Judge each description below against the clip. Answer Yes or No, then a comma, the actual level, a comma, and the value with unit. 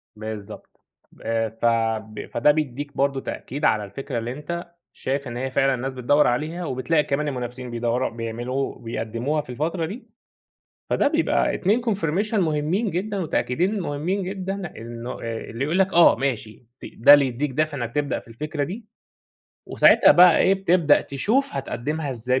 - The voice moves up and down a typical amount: No, wide, 5.9 semitones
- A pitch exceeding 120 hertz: Yes, medium, 140 Hz